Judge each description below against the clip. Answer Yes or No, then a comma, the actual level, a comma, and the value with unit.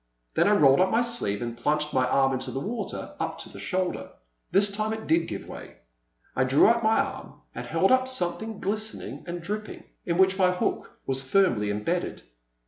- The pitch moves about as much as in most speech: No, wide, 8.1 semitones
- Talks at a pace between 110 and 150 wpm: No, average, 200 wpm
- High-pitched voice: No, medium, 180 Hz